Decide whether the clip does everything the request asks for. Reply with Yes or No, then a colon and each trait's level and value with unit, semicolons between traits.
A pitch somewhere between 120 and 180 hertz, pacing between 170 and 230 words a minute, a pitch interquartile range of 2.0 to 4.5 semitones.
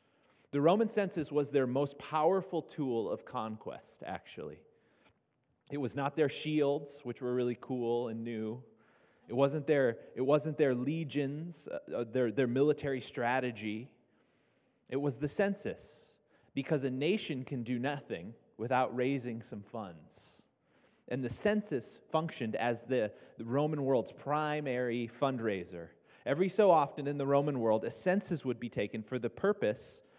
No: medium, 140 Hz; average, 145 wpm; average, 3.9 semitones